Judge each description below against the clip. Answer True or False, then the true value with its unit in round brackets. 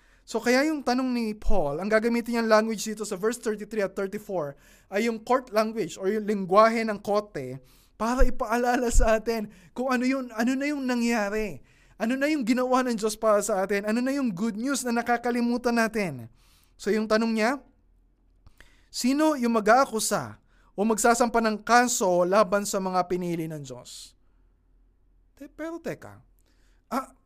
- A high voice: True (220 Hz)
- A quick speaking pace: True (160 wpm)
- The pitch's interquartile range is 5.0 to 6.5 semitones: False (3.9 semitones)